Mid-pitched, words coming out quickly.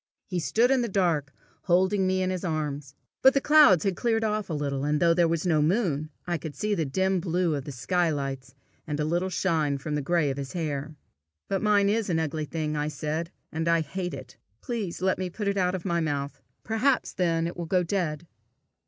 Yes: medium, 170 Hz; fast, 225 wpm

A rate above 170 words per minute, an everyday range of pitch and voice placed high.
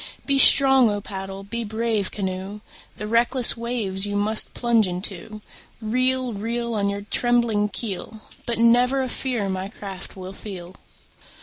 No: average, 145 wpm; average, 3.2 semitones; high, 215 Hz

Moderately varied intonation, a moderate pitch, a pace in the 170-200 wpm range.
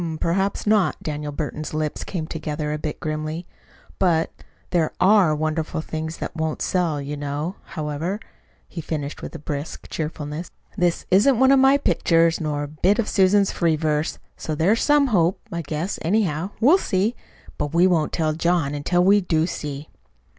Yes: average, 3.6 semitones; medium, 165 Hz; average, 175 wpm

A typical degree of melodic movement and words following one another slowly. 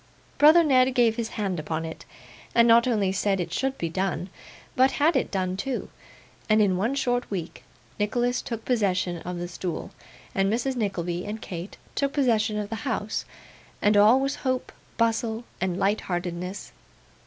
No: average, 4.9 semitones; average, 170 wpm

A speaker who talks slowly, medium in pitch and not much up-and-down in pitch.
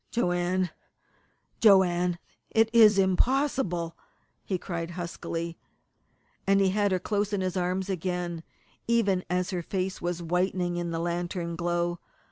Yes: slow, 130 wpm; medium, 180 Hz; narrow, 2.1 semitones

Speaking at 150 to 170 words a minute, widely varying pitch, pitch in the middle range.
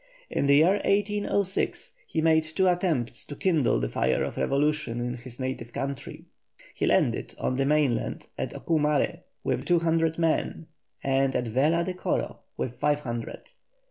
No: average, 160 wpm; average, 4.3 semitones; medium, 150 Hz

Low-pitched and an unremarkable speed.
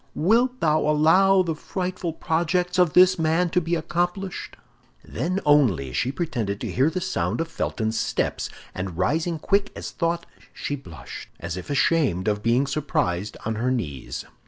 No: medium, 155 Hz; average, 160 wpm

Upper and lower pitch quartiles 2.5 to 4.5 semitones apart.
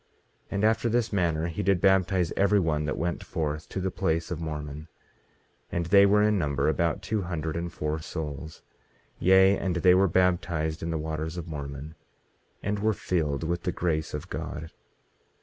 Yes: average, 3.4 semitones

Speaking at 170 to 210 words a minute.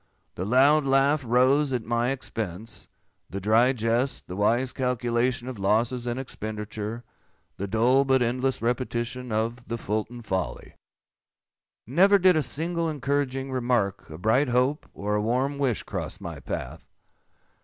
No: average, 145 wpm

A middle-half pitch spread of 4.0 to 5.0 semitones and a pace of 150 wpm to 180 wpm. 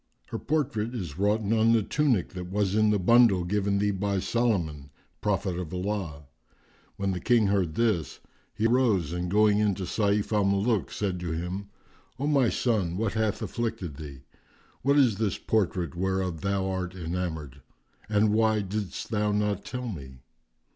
No: average, 3.4 semitones; average, 170 wpm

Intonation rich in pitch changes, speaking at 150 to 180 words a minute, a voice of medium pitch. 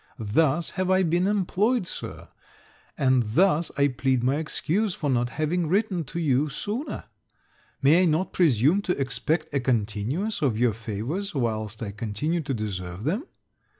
Yes: wide, 6.9 semitones; average, 155 wpm; medium, 150 Hz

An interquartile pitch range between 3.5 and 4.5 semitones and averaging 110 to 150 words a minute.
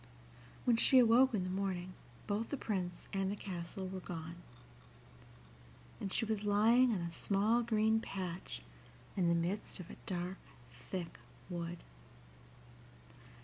Yes: average, 3.8 semitones; average, 140 wpm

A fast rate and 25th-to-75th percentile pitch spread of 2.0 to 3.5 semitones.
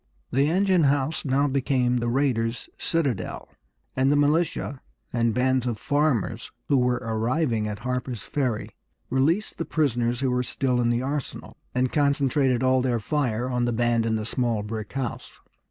No: average, 165 wpm; average, 3.1 semitones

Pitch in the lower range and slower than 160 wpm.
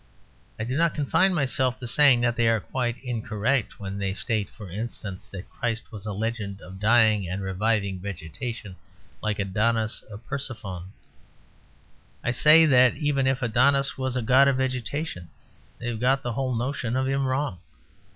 No: low, 120 Hz; average, 170 wpm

